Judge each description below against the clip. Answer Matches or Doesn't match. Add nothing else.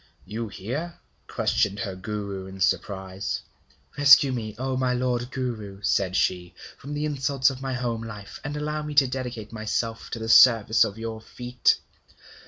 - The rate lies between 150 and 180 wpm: Matches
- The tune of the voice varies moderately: Matches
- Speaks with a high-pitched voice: Doesn't match